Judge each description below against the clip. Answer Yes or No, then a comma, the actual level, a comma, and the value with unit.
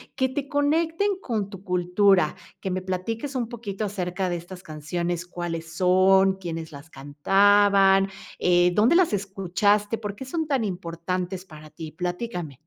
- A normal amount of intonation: Yes, average, 3.3 semitones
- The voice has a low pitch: No, high, 190 Hz